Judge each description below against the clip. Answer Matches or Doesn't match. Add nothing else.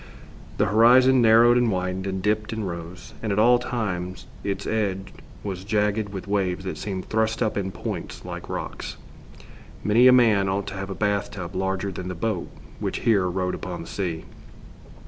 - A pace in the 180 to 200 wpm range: Matches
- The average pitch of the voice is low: Matches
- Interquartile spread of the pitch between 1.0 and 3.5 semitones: Matches